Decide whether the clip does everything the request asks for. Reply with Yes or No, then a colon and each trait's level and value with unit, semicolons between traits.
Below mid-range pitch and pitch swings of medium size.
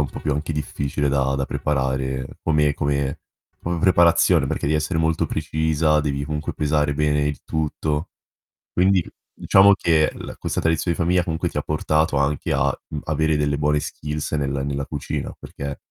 No: very low, 75 Hz; narrow, 1.9 semitones